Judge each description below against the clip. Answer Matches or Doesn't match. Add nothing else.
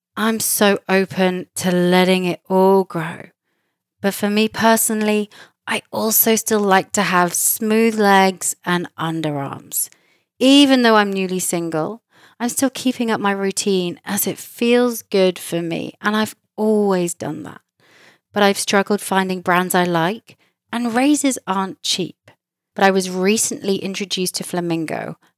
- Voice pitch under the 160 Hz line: Doesn't match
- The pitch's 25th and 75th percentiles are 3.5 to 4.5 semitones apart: Doesn't match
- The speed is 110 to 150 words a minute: Matches